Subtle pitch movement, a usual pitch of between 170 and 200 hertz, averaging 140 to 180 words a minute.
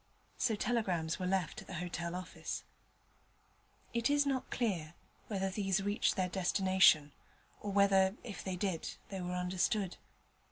Yes: narrow, 2.3 semitones; high, 190 Hz; average, 145 wpm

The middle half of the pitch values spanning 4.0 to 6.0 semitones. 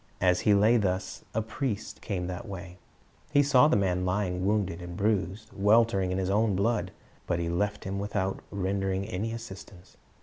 No: average, 2.7 semitones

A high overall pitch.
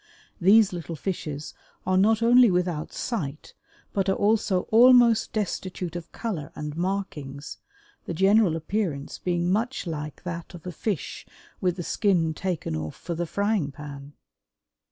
No: medium, 180 Hz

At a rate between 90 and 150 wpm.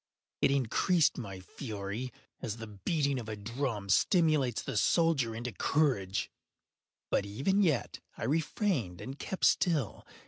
Yes: slow, 135 wpm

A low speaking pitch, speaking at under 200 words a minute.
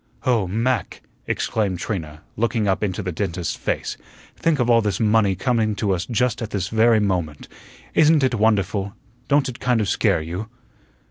Yes: low, 105 Hz; average, 175 wpm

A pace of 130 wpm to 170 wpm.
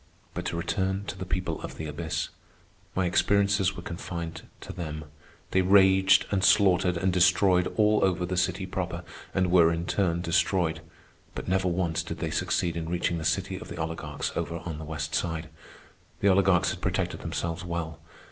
No: average, 180 wpm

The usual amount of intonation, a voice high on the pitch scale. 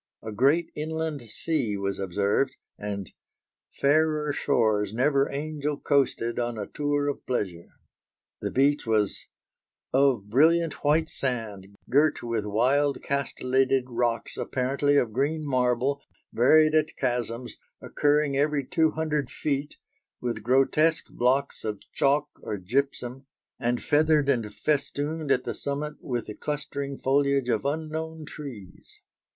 No: average, 3.9 semitones; medium, 140 Hz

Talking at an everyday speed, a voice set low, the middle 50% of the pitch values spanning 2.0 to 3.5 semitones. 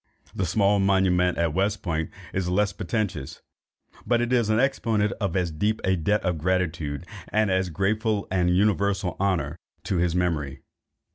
Yes: average, 165 wpm; very low, 95 Hz; average, 2.9 semitones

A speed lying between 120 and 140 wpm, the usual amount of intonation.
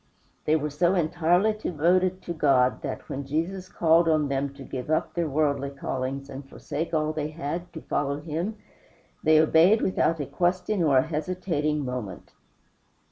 No: average, 165 wpm; average, 3.5 semitones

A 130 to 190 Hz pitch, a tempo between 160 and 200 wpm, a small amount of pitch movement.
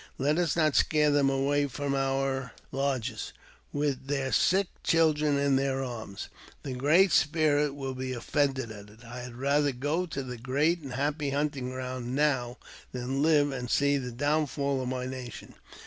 Yes: low, 135 Hz; average, 175 wpm; narrow, 2.3 semitones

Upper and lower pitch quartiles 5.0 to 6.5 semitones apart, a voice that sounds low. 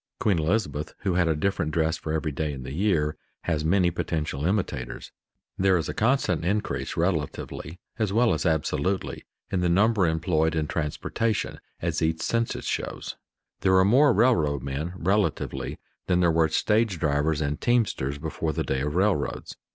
No: average, 4.3 semitones; very low, 85 Hz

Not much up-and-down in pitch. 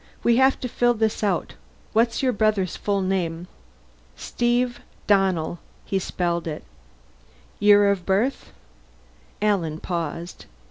No: average, 4.7 semitones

